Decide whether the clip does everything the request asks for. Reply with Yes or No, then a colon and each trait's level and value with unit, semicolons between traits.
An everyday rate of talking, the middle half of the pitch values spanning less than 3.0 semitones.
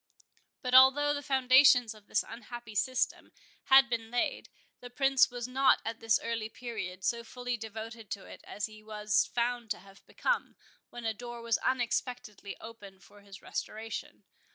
Yes: average, 165 wpm; narrow, 2.6 semitones